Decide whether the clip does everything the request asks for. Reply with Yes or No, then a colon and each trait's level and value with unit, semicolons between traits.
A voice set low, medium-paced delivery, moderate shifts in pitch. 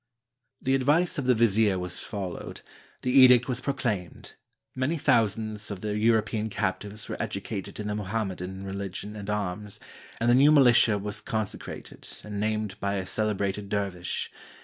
Yes: low, 105 Hz; average, 155 wpm; average, 3.2 semitones